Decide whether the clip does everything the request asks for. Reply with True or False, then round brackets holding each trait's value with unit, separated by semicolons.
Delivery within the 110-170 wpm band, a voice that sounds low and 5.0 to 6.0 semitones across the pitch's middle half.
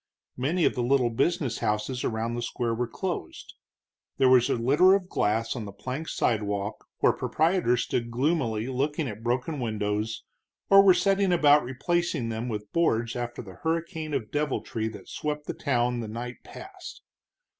True (165 wpm; 125 Hz; 5.6 semitones)